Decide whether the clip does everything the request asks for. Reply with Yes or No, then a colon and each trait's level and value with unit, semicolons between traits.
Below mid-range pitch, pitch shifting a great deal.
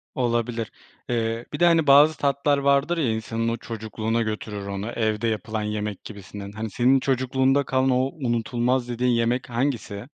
No: low, 120 Hz; average, 3.2 semitones